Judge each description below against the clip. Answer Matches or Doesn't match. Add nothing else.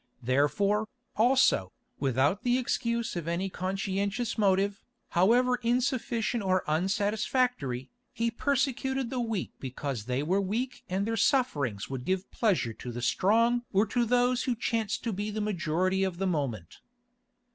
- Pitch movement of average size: Doesn't match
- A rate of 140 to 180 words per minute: Matches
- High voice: Matches